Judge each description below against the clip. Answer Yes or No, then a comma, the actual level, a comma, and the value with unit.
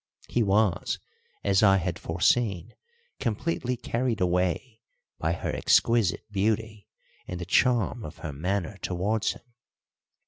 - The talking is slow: Yes, slow, 125 wpm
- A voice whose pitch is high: No, low, 100 Hz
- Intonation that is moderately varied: Yes, average, 3.9 semitones